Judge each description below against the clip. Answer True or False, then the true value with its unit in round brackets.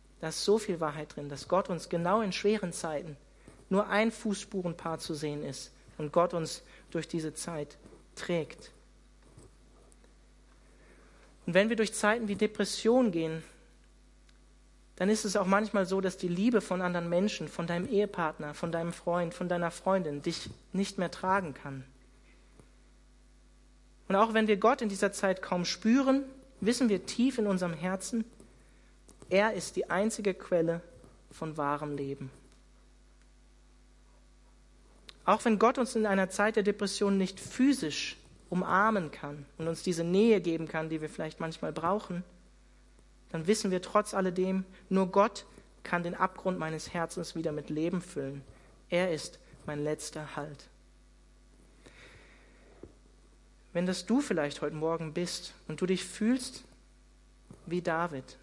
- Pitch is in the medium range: True (180 Hz)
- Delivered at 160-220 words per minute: False (145 wpm)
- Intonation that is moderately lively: True (4.2 semitones)